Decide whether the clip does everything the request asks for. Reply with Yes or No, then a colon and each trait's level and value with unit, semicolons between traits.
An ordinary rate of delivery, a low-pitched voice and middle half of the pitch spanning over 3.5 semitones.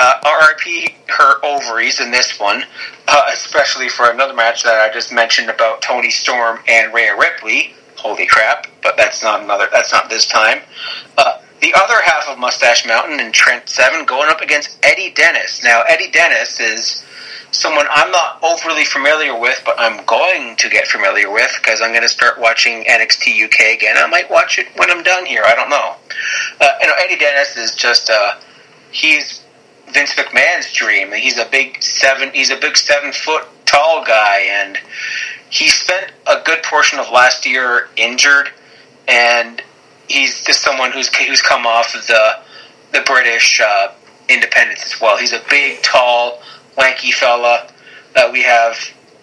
Yes: average, 175 wpm; low, 130 Hz; average, 3.9 semitones